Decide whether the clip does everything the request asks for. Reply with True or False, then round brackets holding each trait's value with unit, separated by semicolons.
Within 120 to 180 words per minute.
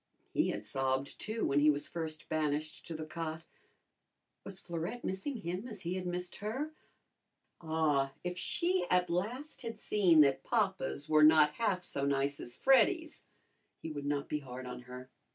True (170 wpm)